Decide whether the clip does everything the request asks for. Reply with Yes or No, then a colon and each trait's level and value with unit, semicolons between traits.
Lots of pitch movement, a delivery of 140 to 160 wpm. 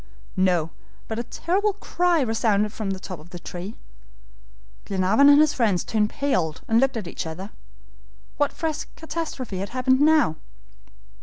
Yes: wide, 7.4 semitones; average, 155 wpm